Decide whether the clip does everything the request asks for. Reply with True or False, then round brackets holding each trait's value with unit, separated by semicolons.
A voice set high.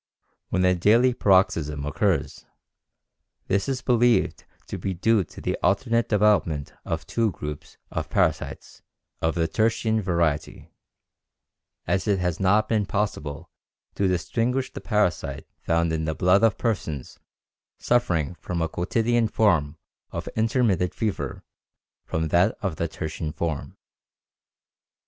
False (95 Hz)